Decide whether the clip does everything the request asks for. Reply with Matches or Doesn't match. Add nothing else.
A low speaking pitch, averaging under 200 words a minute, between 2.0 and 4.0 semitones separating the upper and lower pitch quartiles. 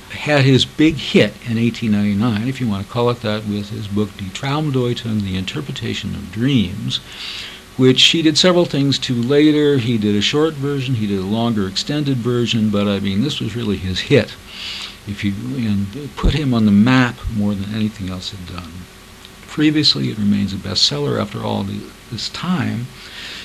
Doesn't match